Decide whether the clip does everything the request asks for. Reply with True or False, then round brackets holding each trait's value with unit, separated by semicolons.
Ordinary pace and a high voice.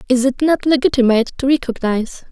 True (155 wpm; 260 Hz)